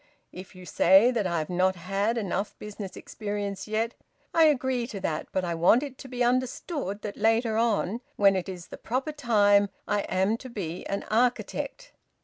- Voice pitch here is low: No, high, 210 Hz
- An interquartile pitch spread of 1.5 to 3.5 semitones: No, average, 4.1 semitones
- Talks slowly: No, average, 185 wpm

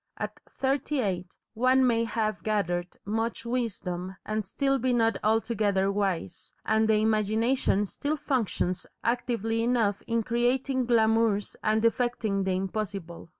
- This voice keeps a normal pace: No, slow, 130 wpm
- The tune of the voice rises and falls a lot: No, average, 3.2 semitones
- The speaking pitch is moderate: No, high, 220 Hz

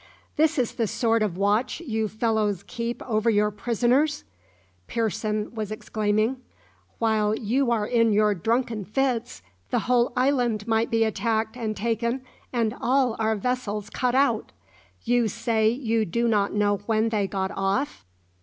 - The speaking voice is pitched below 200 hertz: No, high, 225 Hz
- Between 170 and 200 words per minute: No, average, 150 wpm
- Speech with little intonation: Yes, narrow, 2.3 semitones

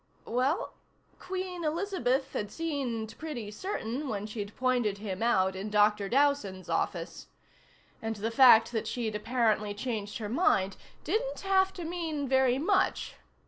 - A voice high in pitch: Yes, high, 245 Hz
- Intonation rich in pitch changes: Yes, wide, 6.5 semitones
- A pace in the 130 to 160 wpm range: Yes, average, 140 wpm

